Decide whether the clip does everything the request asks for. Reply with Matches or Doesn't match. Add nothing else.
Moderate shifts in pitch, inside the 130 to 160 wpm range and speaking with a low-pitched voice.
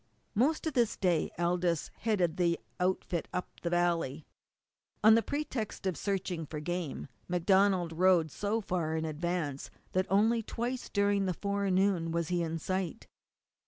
Doesn't match